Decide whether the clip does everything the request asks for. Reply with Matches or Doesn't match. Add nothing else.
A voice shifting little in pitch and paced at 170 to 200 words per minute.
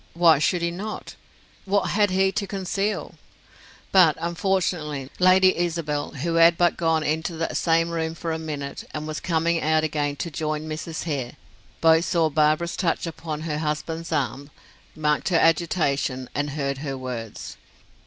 Doesn't match